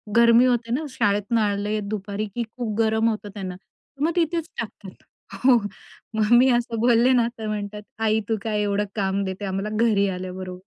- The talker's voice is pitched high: Yes, high, 215 Hz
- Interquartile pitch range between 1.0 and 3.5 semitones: Yes, average, 2.7 semitones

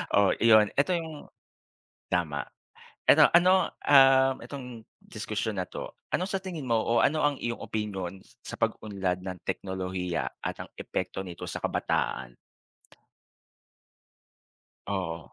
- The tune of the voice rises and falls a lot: Yes, wide, 6.7 semitones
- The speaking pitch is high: No, low, 110 Hz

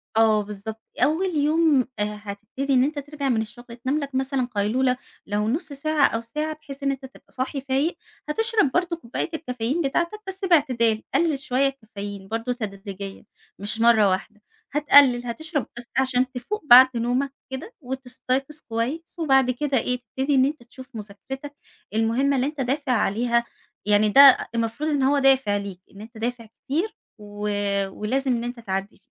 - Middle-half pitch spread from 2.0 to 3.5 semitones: No, average, 4.1 semitones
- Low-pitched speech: No, very high, 255 Hz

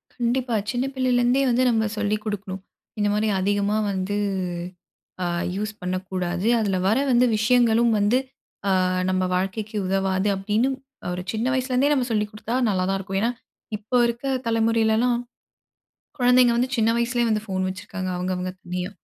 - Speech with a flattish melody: No, average, 3.8 semitones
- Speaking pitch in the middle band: No, high, 215 Hz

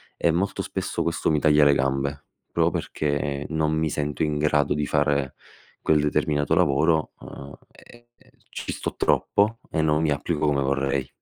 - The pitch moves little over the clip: Yes, narrow, 1.8 semitones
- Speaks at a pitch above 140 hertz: No, very low, 75 Hz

